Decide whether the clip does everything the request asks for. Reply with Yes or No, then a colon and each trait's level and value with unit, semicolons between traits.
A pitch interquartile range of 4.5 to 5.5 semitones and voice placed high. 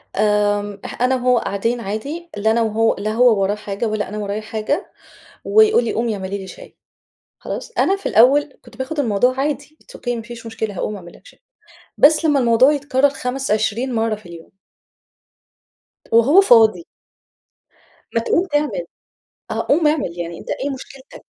Yes: average, 5.0 semitones; high, 235 Hz